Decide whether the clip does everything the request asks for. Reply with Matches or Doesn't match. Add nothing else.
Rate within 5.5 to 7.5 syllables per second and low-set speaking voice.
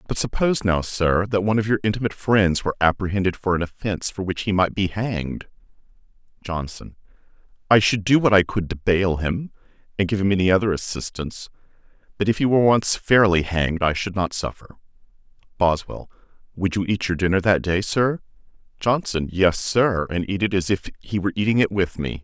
Matches